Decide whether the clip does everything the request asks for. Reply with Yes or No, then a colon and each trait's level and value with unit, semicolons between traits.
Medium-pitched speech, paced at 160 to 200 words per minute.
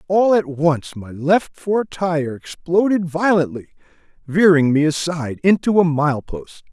No: medium, 165 Hz; average, 145 wpm